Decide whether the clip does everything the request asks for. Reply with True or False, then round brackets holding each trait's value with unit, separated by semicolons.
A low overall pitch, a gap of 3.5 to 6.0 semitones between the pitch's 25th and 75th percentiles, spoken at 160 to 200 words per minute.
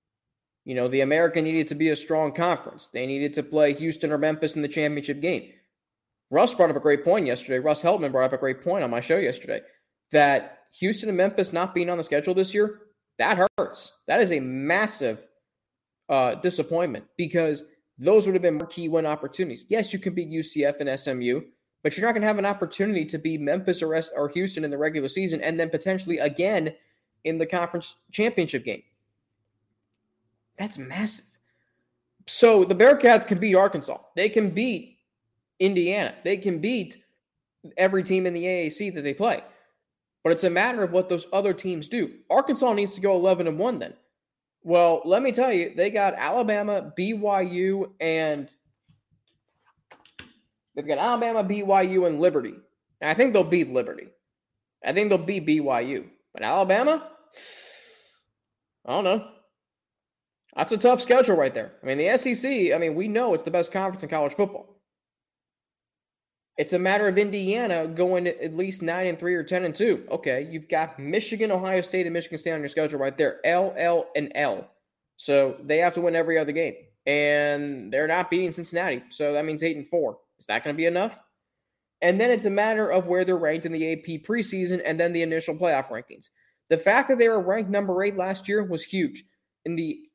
False (175 Hz; 4.4 semitones; 190 wpm)